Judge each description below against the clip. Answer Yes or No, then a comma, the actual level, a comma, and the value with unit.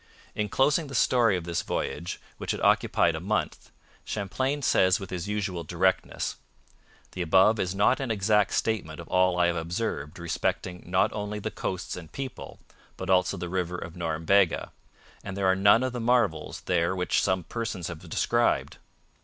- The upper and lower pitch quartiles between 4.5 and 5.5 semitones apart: No, average, 3.4 semitones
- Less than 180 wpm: Yes, average, 170 wpm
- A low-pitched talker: Yes, very low, 95 Hz